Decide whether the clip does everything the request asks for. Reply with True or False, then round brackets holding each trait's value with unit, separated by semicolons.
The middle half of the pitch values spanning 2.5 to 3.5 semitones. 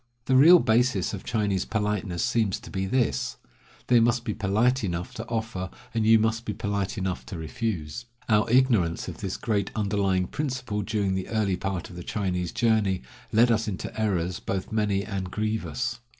True (3.1 semitones)